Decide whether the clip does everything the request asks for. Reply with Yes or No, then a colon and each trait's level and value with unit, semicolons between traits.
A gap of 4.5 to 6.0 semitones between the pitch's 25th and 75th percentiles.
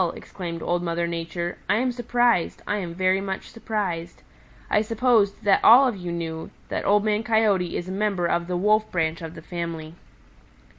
No: average, 3.9 semitones